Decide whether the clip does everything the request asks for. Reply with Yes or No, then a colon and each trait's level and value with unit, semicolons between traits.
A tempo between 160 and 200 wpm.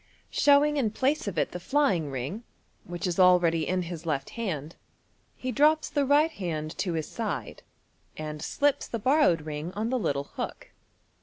Yes: average, 175 wpm